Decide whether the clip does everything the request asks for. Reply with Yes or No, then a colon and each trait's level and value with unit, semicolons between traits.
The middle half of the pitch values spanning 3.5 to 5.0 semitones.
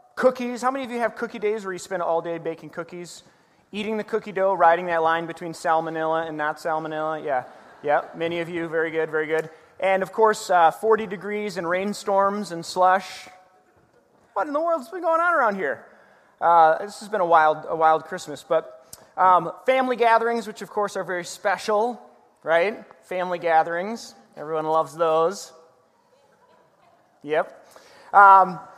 Yes: average, 4.3 semitones